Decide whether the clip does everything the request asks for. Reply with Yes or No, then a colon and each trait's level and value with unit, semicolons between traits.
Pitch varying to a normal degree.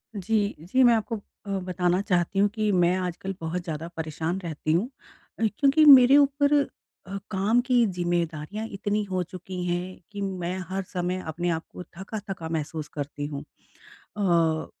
Yes: average, 3.5 semitones